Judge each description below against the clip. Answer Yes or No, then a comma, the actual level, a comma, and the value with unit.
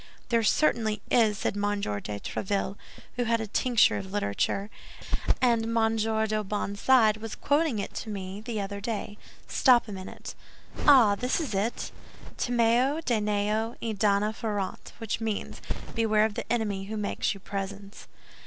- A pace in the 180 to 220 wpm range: No, average, 155 wpm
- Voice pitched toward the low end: No, high, 215 Hz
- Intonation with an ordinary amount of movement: No, narrow, 2.3 semitones